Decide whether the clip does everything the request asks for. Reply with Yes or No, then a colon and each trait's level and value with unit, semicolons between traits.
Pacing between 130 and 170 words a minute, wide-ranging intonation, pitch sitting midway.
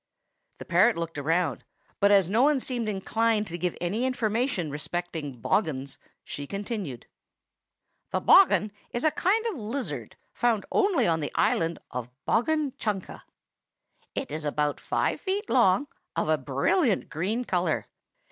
No: average, 145 wpm; wide, 7.0 semitones; high, 200 Hz